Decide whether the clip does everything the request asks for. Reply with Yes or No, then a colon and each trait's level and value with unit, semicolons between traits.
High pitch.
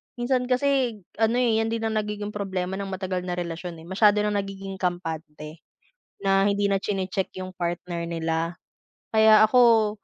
Yes: high, 195 Hz